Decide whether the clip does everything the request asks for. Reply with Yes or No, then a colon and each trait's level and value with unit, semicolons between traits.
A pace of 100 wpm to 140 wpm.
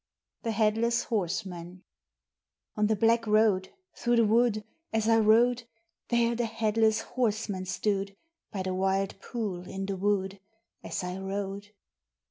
Yes: slow, 135 wpm